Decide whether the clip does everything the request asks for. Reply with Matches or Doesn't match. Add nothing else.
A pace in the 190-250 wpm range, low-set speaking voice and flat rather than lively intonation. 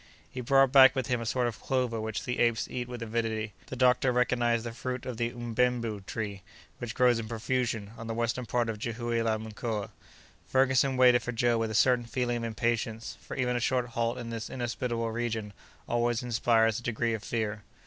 Matches